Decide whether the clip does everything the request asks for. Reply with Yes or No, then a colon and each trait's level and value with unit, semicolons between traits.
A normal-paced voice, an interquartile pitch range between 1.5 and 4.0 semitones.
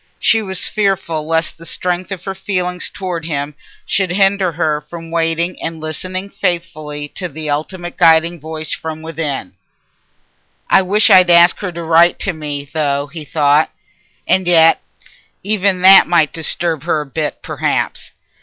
Yes: average, 155 wpm; average, 2.8 semitones